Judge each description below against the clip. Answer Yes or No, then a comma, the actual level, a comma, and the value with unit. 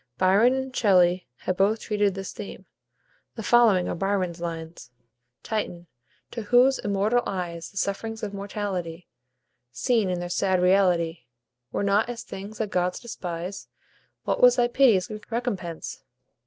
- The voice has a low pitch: No, high, 195 Hz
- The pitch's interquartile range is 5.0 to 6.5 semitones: No, average, 3.8 semitones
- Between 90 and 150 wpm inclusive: Yes, average, 140 wpm